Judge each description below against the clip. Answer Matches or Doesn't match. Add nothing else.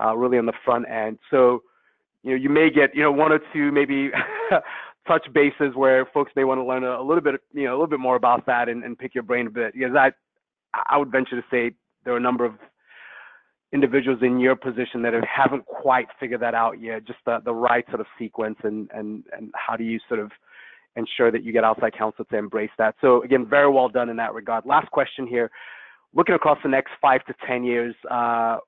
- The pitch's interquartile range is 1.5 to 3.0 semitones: Matches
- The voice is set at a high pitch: Doesn't match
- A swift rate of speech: Matches